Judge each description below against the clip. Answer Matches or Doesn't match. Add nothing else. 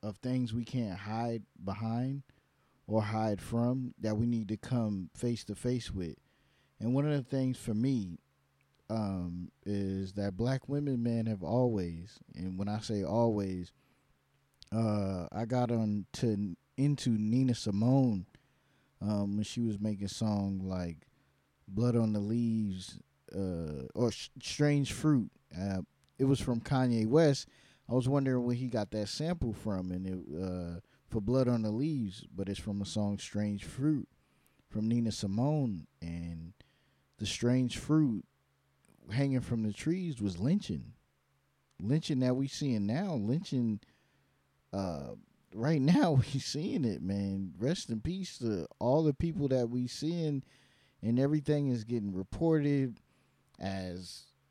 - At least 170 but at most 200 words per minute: Doesn't match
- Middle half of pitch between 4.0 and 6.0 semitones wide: Matches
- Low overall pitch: Matches